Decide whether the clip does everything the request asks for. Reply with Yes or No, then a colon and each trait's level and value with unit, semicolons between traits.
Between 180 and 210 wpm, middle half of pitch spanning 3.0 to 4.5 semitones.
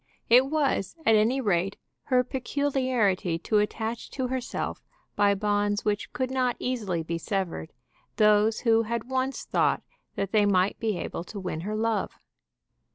No: average, 155 wpm; average, 4.1 semitones